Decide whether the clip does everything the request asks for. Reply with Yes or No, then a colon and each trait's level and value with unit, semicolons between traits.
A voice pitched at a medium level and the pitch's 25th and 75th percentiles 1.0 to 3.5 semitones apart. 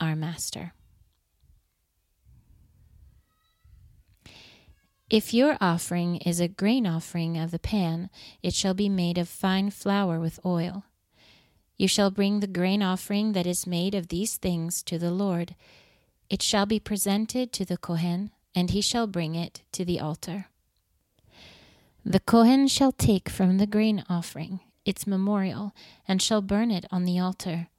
Yes: medium, 180 Hz; average, 3.2 semitones